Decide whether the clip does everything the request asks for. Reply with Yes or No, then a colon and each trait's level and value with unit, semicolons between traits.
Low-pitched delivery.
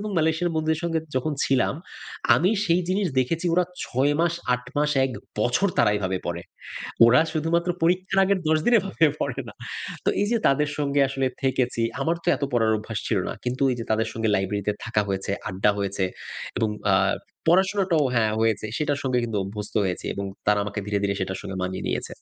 Yes: low, 130 Hz